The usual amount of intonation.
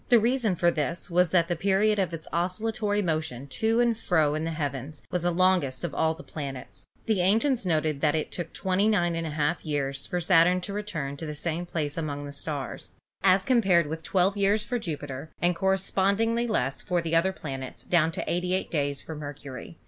Yes: average, 4.2 semitones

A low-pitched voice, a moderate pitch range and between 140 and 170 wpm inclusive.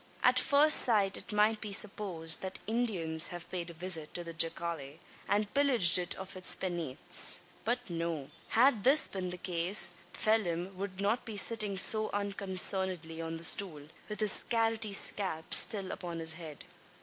No: high, 190 Hz; average, 4.2 semitones; average, 165 wpm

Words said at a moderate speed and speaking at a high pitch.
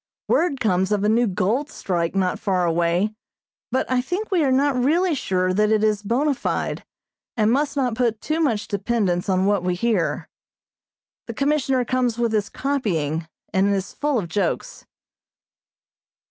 Yes: average, 165 wpm; high, 220 Hz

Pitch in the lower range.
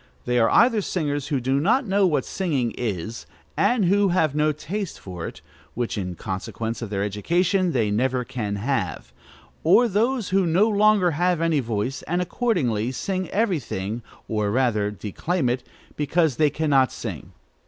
No: medium, 145 Hz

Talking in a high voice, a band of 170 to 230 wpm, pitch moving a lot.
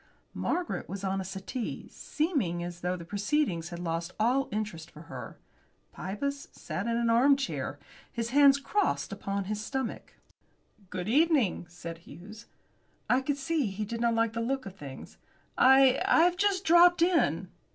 No: high, 230 Hz; average, 160 wpm; wide, 7.2 semitones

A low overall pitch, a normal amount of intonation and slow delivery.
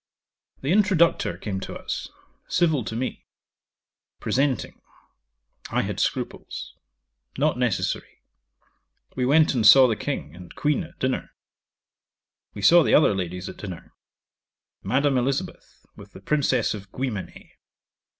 No: low, 130 Hz; wide, 6.3 semitones; slow, 125 wpm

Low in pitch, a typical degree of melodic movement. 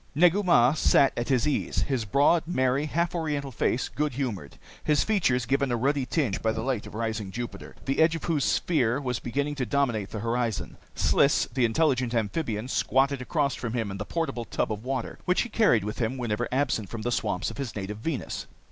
Yes: low, 130 Hz; average, 4.2 semitones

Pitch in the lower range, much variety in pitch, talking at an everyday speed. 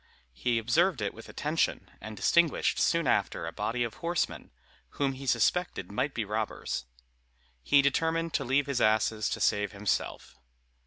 Yes: low, 120 Hz; wide, 5.7 semitones; average, 155 wpm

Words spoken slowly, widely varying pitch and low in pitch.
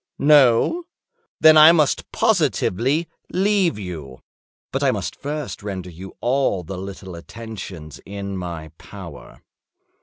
Yes: slow, 120 wpm; wide, 8.9 semitones; low, 100 Hz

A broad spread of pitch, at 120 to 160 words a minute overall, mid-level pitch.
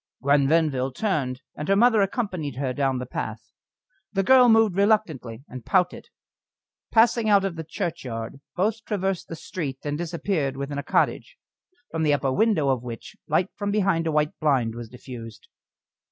No: wide, 6.8 semitones; average, 170 wpm; medium, 155 Hz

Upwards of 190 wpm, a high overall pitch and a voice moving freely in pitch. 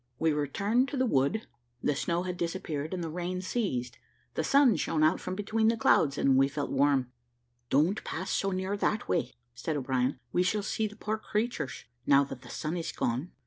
No: average, 200 wpm; medium, 170 Hz; wide, 6.5 semitones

